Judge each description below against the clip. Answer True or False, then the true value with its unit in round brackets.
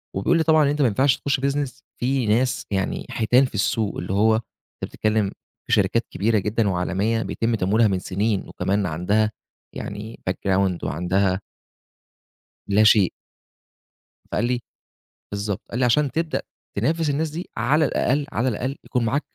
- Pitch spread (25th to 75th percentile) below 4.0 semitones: False (5.0 semitones)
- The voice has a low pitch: True (110 Hz)